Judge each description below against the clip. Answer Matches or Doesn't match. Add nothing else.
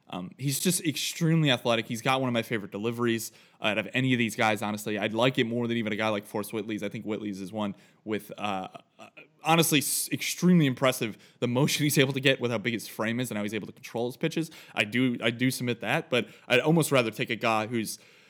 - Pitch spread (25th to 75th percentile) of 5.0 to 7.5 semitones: Doesn't match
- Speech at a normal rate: Doesn't match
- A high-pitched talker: Doesn't match